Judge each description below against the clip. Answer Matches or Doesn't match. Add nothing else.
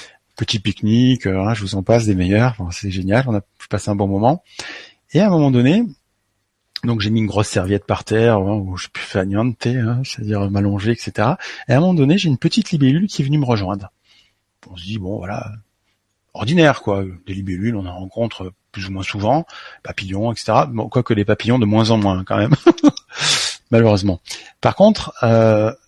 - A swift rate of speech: Doesn't match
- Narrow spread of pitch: Doesn't match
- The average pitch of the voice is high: Doesn't match